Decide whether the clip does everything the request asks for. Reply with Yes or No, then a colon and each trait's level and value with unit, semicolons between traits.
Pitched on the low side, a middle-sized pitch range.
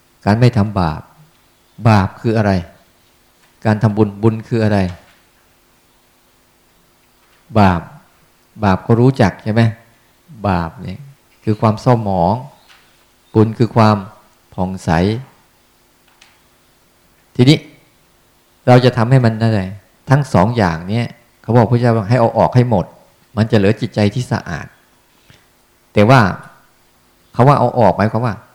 Yes: low, 110 Hz; average, 4.2 semitones